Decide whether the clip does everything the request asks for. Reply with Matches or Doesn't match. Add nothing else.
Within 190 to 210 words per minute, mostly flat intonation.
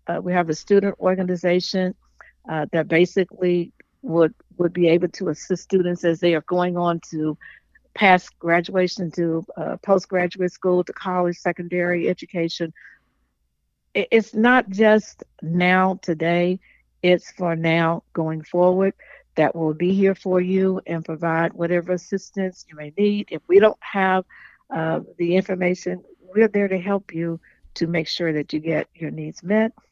Doesn't match